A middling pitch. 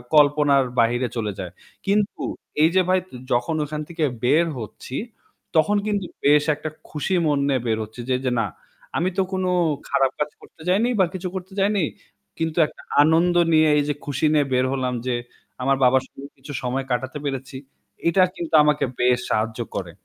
Yes: medium, 145 Hz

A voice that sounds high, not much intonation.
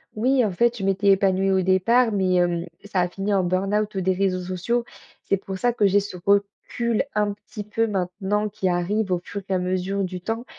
Yes: high, 195 Hz; narrow, 2.2 semitones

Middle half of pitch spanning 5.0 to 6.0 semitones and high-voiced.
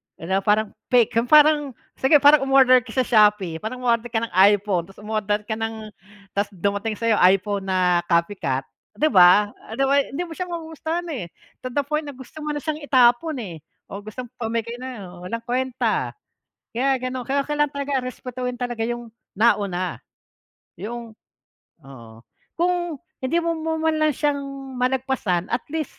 Yes: average, 5.3 semitones; high, 240 Hz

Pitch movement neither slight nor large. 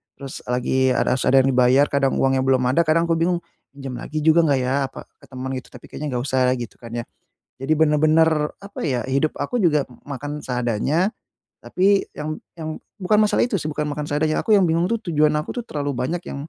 Yes: average, 3.6 semitones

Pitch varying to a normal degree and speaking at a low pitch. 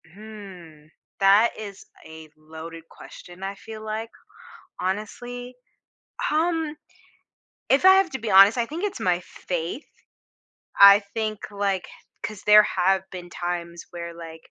No: average, 4.3 semitones; high, 200 Hz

